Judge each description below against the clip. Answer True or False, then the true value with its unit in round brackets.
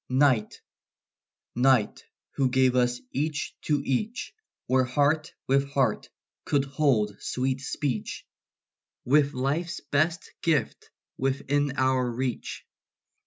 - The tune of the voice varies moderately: False (2.3 semitones)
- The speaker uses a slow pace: True (100 wpm)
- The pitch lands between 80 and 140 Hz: True (135 Hz)